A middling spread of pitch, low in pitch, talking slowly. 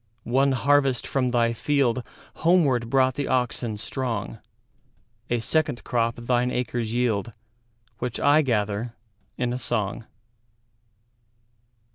No: narrow, 2.2 semitones; low, 120 Hz; slow, 95 wpm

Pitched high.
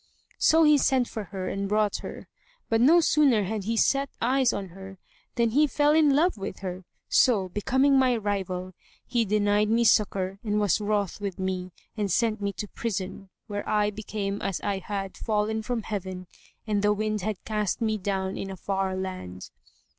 Yes: high, 210 Hz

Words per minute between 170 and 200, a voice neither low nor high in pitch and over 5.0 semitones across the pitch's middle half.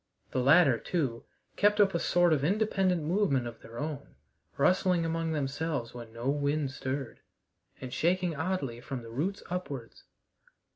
No: average, 150 wpm; medium, 150 Hz; wide, 5.5 semitones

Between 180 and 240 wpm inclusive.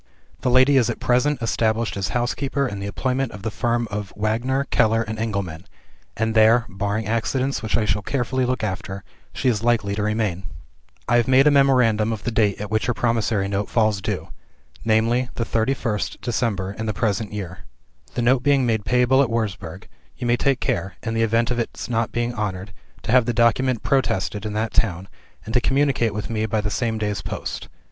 Yes: average, 200 wpm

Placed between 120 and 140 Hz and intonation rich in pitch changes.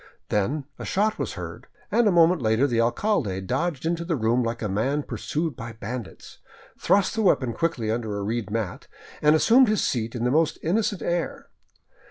Yes: low, 135 Hz; wide, 7.1 semitones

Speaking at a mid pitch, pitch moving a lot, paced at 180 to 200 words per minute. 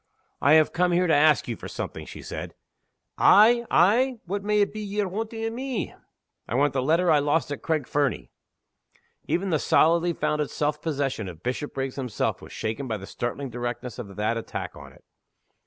Yes: medium, 150 Hz; wide, 7.1 semitones; average, 190 wpm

